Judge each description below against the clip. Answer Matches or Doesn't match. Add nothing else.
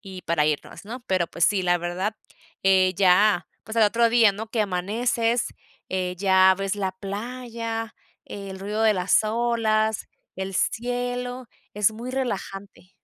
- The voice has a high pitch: Matches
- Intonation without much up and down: Doesn't match